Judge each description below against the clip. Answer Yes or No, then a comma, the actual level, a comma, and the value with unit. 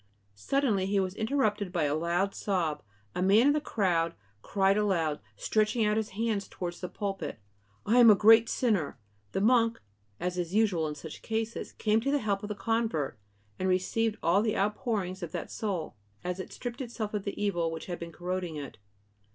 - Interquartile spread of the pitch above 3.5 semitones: Yes, average, 4.1 semitones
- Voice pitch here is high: Yes, high, 200 Hz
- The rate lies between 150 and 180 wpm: No, average, 195 wpm